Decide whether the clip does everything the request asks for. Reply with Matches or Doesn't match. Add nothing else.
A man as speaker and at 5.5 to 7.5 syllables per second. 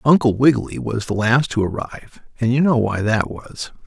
Doesn't match